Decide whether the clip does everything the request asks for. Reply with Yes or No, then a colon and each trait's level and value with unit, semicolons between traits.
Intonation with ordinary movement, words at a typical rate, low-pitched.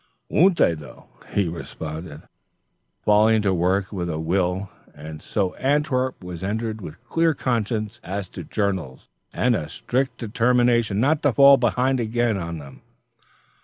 No: wide, 5.9 semitones; average, 145 wpm; low, 105 Hz